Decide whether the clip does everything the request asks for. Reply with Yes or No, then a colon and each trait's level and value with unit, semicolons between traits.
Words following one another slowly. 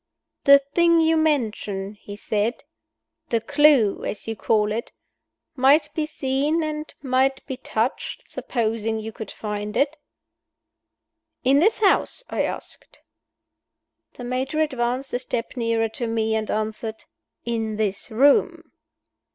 Yes: slow, 130 wpm